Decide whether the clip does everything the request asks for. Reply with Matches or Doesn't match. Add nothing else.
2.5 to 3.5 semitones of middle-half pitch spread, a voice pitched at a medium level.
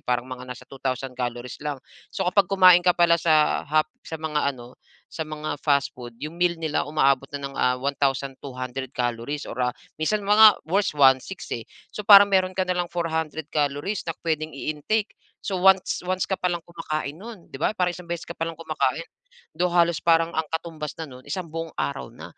Doesn't match